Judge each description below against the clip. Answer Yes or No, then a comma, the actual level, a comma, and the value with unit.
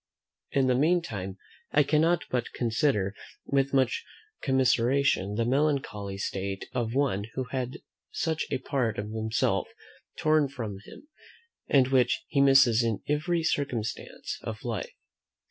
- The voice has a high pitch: No, low, 130 Hz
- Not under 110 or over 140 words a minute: Yes, slow, 135 wpm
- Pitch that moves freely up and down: No, average, 4.2 semitones